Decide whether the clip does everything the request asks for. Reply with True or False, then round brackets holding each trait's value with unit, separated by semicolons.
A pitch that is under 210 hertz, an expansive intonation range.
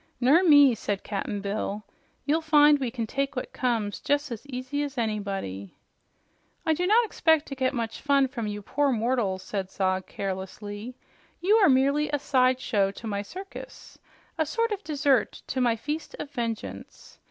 False (255 Hz; 5.8 semitones)